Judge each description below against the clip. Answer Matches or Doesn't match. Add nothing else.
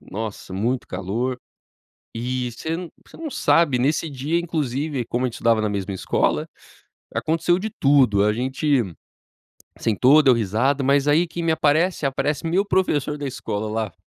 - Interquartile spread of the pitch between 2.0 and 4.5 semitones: Doesn't match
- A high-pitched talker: Doesn't match